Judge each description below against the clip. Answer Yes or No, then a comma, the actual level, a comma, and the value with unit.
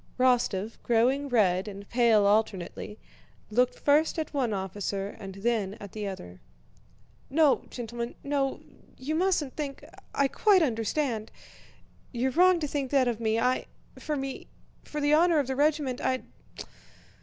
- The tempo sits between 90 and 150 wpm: Yes, average, 145 wpm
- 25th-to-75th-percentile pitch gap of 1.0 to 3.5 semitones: No, average, 5.1 semitones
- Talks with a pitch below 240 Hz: No, very high, 250 Hz